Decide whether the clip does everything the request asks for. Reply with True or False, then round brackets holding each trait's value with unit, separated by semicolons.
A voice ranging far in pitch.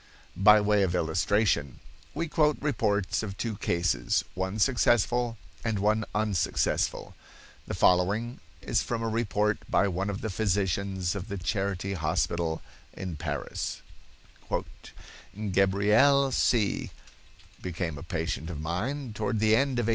False (3.7 semitones)